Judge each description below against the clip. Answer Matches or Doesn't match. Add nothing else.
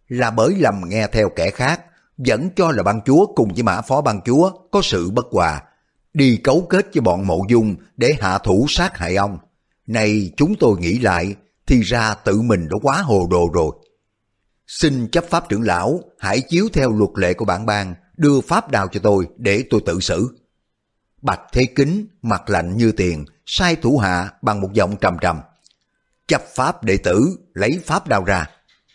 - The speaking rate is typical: Matches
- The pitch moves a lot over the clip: Matches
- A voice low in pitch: Matches